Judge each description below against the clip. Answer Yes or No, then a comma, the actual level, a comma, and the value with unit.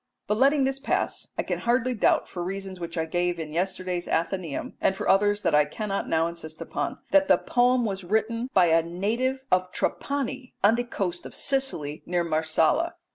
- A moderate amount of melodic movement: No, wide, 6.1 semitones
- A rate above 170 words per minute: Yes, average, 190 wpm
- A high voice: Yes, high, 195 Hz